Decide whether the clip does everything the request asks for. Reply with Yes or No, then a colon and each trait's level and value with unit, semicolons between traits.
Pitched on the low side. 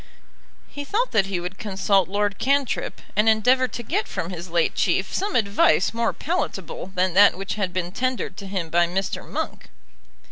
No: high, 200 Hz